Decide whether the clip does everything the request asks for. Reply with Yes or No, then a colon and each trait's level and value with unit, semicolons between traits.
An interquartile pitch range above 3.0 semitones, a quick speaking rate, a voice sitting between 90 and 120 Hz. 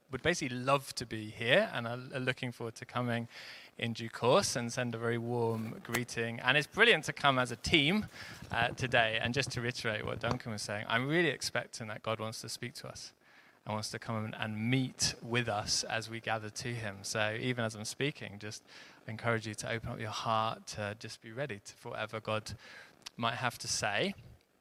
No: narrow, 2.4 semitones; fast, 215 wpm; low, 115 Hz